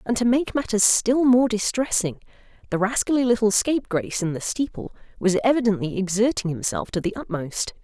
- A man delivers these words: No, female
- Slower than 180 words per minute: Yes, average, 170 wpm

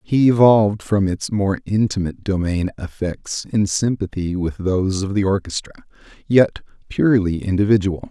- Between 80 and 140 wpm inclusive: Yes, slow, 135 wpm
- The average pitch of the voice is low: Yes, low, 100 Hz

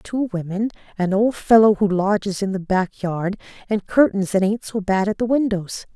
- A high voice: Yes, high, 205 Hz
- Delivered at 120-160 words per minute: No, average, 200 wpm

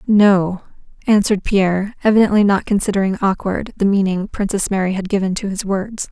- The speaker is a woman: Yes, female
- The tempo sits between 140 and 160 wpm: Yes, average, 155 wpm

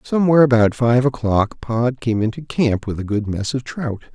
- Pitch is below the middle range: Yes, low, 120 Hz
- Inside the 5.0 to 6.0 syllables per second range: Yes, 5.1 syllables/s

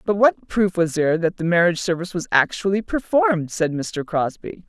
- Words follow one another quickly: No, average, 190 wpm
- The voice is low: No, medium, 175 Hz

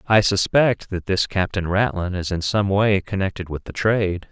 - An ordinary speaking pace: Yes, average, 195 wpm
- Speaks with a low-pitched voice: Yes, very low, 95 Hz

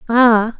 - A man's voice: No, female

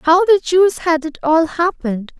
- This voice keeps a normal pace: Yes, average, 190 wpm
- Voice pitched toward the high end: Yes, very high, 325 Hz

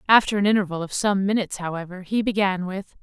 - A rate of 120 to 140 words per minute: No, average, 200 wpm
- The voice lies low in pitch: No, high, 195 Hz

